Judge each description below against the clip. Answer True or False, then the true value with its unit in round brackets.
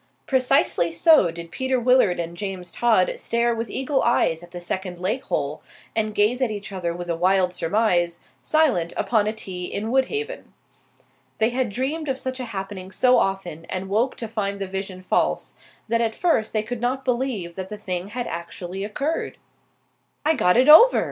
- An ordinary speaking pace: True (180 wpm)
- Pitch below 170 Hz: False (210 Hz)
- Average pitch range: False (5.7 semitones)